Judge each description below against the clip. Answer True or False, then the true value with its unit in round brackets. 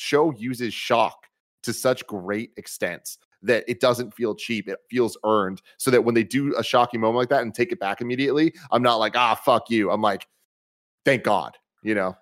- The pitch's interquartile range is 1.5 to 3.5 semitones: True (3.1 semitones)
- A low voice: True (115 Hz)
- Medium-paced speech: False (210 wpm)